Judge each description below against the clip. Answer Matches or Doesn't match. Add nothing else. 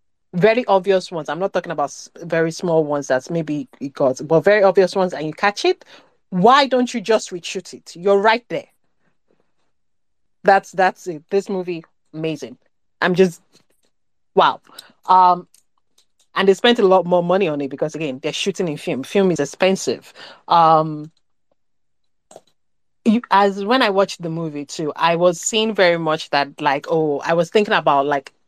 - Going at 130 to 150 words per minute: Doesn't match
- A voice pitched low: Doesn't match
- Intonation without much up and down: Doesn't match